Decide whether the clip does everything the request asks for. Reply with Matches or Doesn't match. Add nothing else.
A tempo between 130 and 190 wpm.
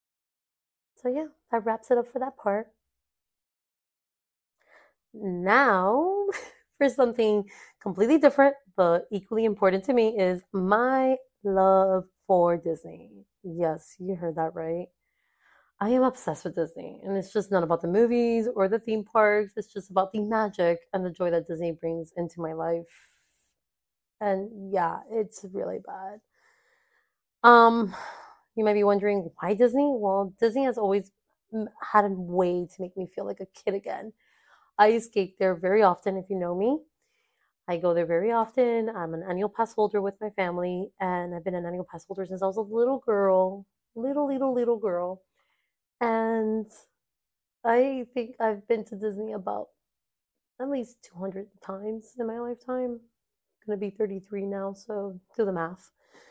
Matches